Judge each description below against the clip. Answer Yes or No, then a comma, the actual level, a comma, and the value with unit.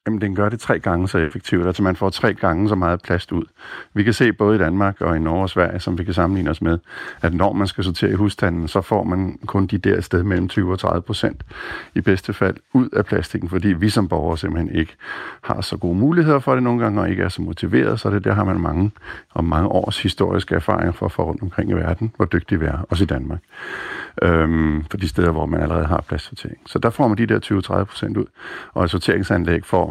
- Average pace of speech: No, fast, 255 wpm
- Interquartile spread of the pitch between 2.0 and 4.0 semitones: Yes, average, 3.4 semitones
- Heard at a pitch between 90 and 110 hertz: Yes, very low, 95 Hz